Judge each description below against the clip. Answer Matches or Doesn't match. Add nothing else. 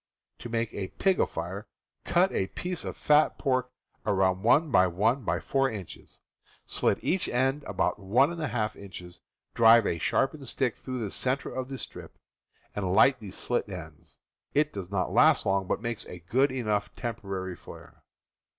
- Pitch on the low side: Matches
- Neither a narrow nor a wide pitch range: Doesn't match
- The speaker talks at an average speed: Matches